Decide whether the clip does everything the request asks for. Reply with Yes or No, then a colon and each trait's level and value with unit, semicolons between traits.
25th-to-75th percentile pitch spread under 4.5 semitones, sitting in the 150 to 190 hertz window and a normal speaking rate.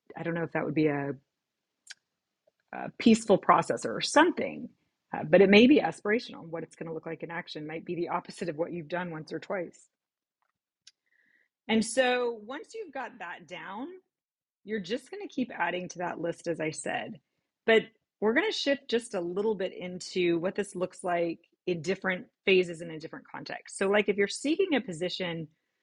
No: average, 5.3 semitones; medium, 185 Hz; average, 195 wpm